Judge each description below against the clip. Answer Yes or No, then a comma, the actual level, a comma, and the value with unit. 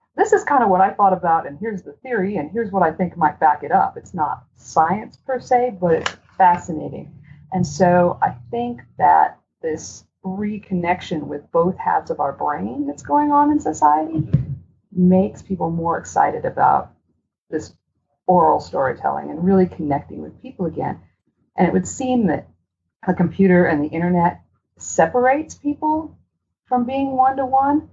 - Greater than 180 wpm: No, average, 170 wpm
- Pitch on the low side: No, medium, 185 Hz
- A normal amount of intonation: No, wide, 7.8 semitones